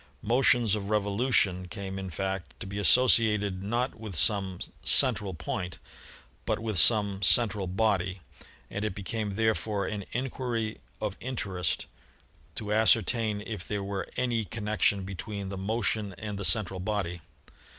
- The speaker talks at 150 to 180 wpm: No, average, 140 wpm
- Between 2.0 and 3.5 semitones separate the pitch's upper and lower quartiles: Yes, narrow, 2.6 semitones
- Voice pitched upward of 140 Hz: No, low, 105 Hz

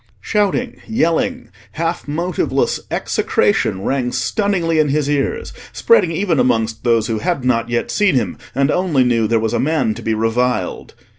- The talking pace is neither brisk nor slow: Yes, average, 160 wpm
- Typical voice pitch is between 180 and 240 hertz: No, medium, 140 Hz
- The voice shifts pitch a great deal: Yes, wide, 7.1 semitones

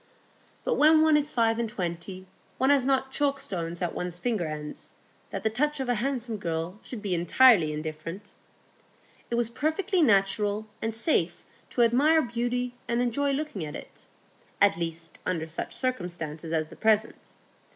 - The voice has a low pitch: No, high, 220 Hz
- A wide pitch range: Yes, wide, 7.2 semitones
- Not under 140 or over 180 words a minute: Yes, average, 160 wpm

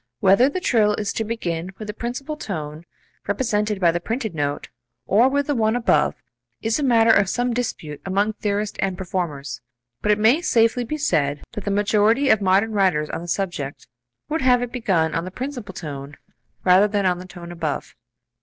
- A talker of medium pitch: No, high, 205 Hz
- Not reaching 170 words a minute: No, average, 190 wpm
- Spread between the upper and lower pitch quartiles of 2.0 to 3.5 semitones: No, average, 5.1 semitones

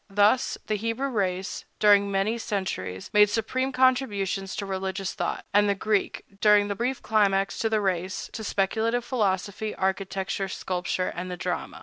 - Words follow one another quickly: No, average, 155 wpm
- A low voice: No, high, 200 Hz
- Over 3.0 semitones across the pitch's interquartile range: No, narrow, 2.4 semitones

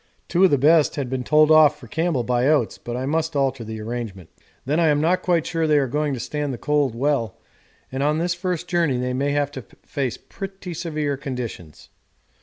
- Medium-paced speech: No, fast, 215 wpm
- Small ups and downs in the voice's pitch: No, average, 4.1 semitones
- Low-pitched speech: No, medium, 145 Hz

